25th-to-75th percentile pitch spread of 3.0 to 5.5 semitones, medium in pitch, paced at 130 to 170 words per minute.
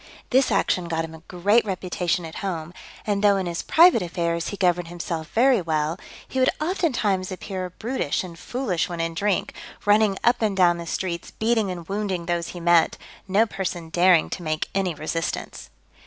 No: average, 3.5 semitones; medium, 180 Hz; average, 185 wpm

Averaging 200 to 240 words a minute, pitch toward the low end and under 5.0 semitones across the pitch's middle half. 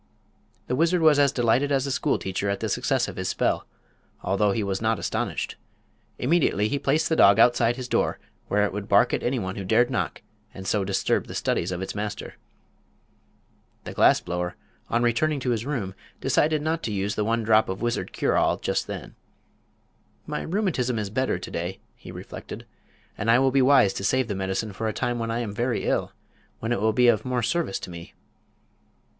Yes: fast, 205 wpm; low, 115 Hz; average, 4.5 semitones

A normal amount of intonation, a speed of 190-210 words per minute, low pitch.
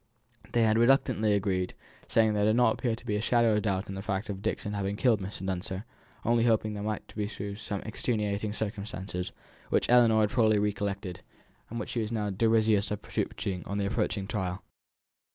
No: narrow, 2.0 semitones; average, 195 wpm; low, 105 Hz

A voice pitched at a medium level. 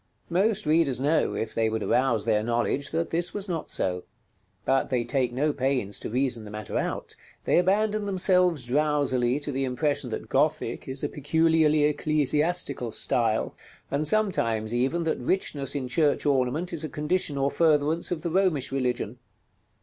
Yes: medium, 145 Hz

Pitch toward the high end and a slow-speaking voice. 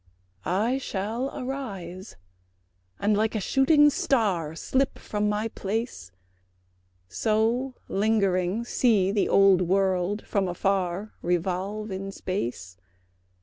Yes: high, 200 Hz; slow, 105 wpm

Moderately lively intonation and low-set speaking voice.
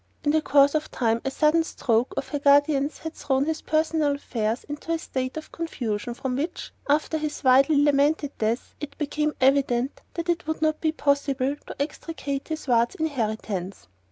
No: average, 3.2 semitones; very high, 285 Hz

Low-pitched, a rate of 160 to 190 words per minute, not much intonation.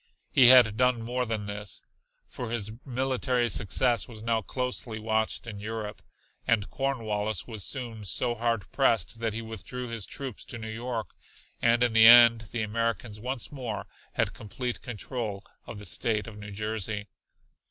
Yes: low, 115 Hz; average, 165 wpm; narrow, 2.3 semitones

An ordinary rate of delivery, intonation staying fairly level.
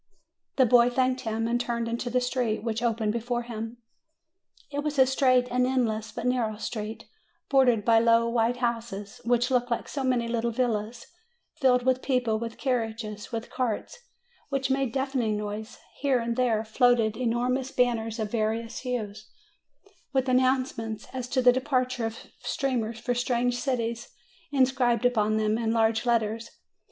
Yes: average, 160 wpm; narrow, 2.1 semitones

